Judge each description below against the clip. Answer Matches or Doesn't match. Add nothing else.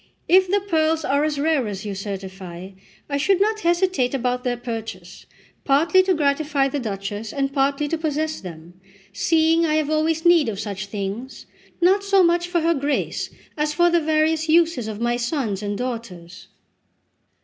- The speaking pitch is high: Matches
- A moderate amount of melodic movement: Doesn't match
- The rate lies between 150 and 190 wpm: Matches